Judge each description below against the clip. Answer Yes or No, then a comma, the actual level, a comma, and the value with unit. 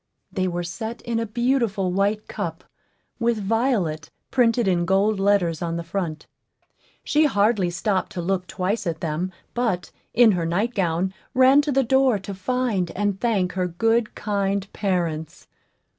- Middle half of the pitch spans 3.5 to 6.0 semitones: Yes, average, 4.3 semitones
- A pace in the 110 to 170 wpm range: Yes, average, 155 wpm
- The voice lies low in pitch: No, high, 200 Hz